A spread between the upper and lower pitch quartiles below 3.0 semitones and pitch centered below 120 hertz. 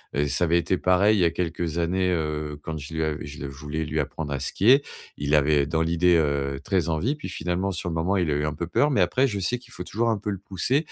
No: average, 3.8 semitones; very low, 85 Hz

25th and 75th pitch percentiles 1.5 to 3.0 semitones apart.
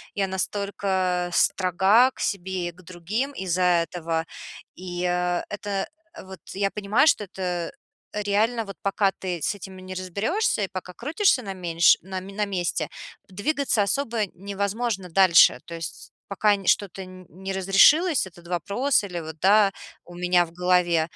Yes: narrow, 2.4 semitones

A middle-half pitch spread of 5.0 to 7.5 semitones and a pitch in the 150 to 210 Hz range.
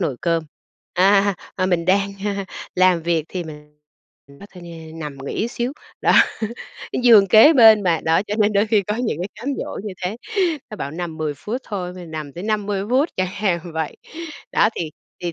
No: average, 4.2 semitones; medium, 185 Hz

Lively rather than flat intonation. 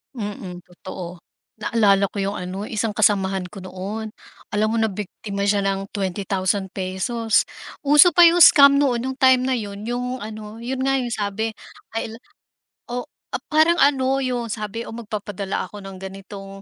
No: average, 3.9 semitones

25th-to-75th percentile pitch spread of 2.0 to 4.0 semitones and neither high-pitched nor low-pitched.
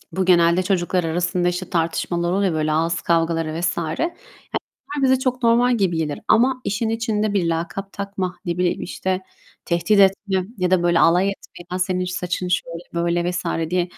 Yes: narrow, 2.5 semitones; medium, 180 Hz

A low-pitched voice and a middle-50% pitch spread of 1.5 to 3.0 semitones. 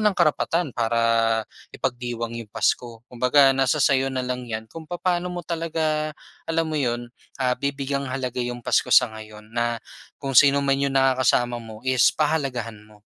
No: low, 130 Hz; average, 3.7 semitones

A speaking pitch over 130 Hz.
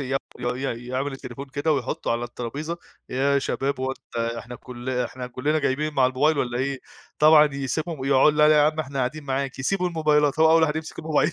Yes: medium, 140 Hz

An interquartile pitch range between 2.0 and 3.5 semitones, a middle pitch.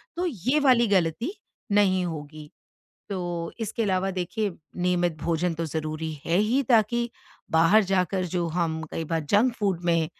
No: average, 4.3 semitones; medium, 180 Hz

